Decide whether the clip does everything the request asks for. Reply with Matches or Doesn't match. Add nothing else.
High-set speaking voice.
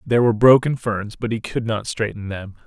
Doesn't match